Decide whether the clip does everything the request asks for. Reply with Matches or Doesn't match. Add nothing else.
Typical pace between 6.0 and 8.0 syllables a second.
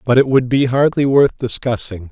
Doesn't match